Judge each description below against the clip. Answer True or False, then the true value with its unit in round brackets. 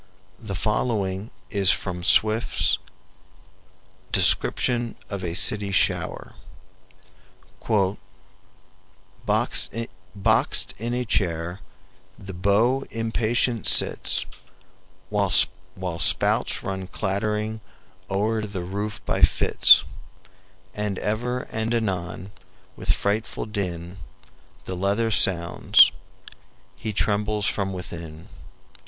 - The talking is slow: True (85 wpm)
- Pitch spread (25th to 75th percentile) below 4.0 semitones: True (2.9 semitones)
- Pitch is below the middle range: True (100 Hz)